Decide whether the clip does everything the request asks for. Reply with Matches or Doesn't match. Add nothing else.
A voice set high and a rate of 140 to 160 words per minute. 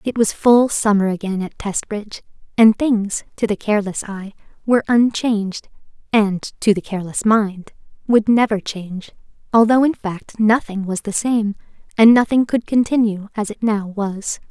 Matches